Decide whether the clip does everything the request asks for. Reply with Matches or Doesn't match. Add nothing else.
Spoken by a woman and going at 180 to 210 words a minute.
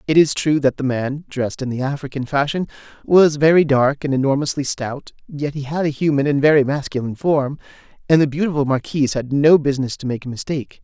Doesn't match